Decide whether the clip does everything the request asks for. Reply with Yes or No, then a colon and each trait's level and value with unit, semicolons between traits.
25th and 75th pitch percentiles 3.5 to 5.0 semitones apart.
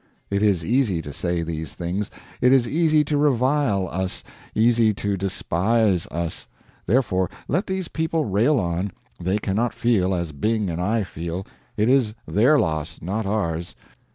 No: wide, 5.4 semitones